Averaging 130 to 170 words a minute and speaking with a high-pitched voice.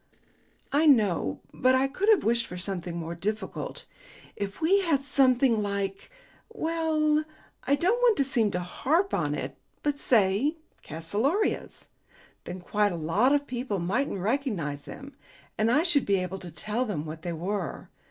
Yes: average, 160 wpm; high, 230 Hz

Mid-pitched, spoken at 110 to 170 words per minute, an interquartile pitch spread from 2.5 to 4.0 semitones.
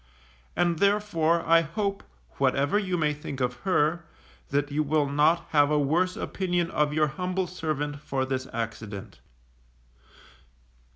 Yes: medium, 155 Hz; slow, 135 wpm; average, 3.6 semitones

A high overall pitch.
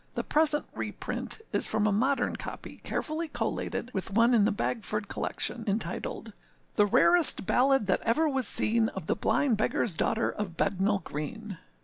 Yes: high, 220 Hz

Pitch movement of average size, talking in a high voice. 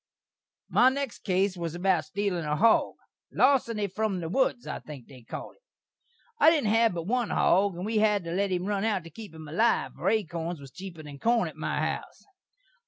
Yes: average, 4.8 semitones; high, 195 Hz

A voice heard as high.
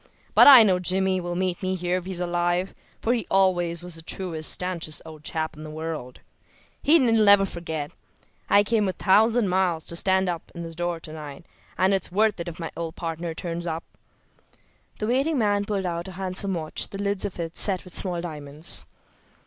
No: medium, 180 Hz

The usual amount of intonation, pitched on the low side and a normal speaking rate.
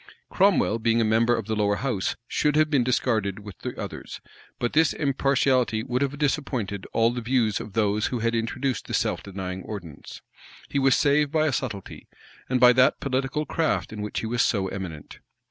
Yes: average, 4.5 semitones; low, 120 Hz; average, 195 wpm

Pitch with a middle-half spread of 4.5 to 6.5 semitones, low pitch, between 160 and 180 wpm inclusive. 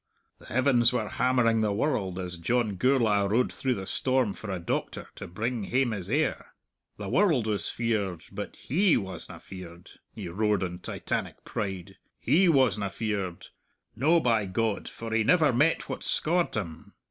Yes: average, 4.8 semitones; low, 110 Hz; average, 165 wpm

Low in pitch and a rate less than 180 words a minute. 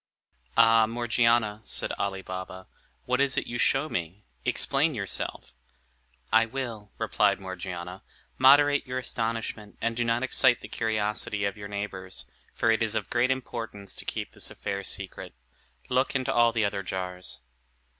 Yes: low, 110 Hz; average, 155 wpm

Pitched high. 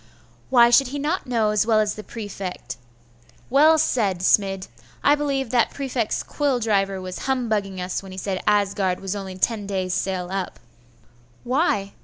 Yes: high, 210 Hz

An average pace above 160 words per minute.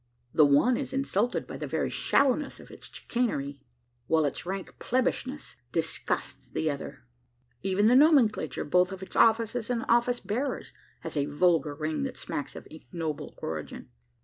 No: average, 155 wpm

